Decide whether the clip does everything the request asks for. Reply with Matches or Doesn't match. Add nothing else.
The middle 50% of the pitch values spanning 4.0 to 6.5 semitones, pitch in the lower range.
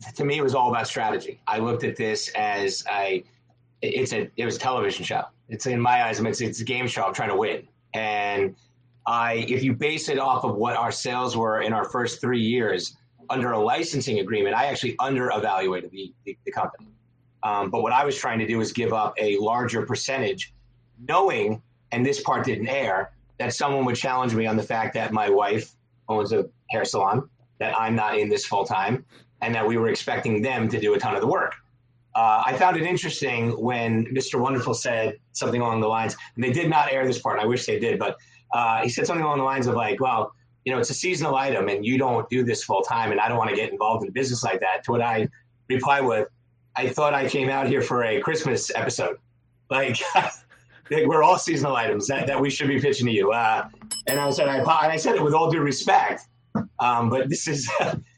Doesn't match